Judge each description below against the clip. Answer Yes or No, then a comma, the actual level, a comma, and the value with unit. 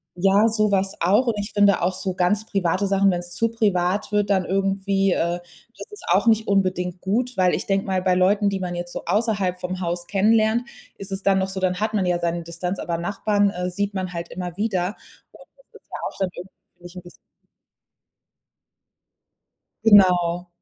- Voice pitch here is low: No, high, 190 Hz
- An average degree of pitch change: No, narrow, 2.3 semitones